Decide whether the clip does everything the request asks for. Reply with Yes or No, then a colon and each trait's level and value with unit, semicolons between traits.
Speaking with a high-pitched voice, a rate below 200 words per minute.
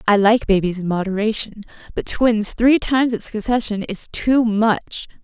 Yes: high, 215 Hz; average, 160 wpm